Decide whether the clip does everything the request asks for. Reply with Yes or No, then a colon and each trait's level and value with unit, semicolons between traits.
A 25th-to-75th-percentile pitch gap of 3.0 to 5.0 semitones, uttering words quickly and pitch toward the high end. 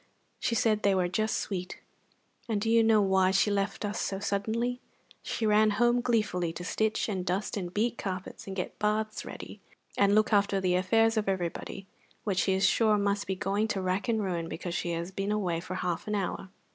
No: narrow, 2.6 semitones; fast, 210 wpm; high, 200 Hz